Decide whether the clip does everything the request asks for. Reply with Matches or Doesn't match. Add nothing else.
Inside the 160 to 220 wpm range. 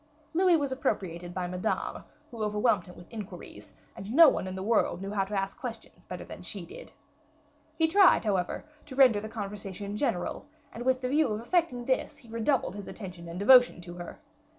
Matches